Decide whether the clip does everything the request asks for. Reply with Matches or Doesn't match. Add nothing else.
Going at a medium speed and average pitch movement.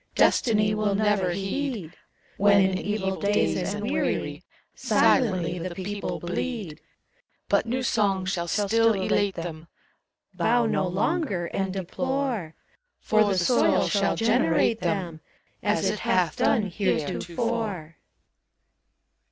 Doesn't match